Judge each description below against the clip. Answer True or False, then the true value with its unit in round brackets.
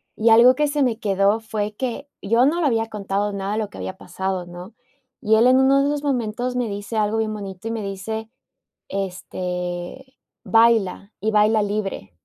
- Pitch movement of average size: True (3.2 semitones)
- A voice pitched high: True (215 Hz)